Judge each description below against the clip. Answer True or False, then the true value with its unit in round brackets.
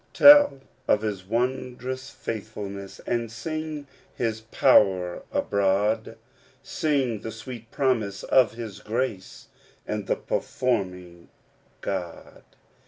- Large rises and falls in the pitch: False (4.3 semitones)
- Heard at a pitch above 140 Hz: False (110 Hz)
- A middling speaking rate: False (100 wpm)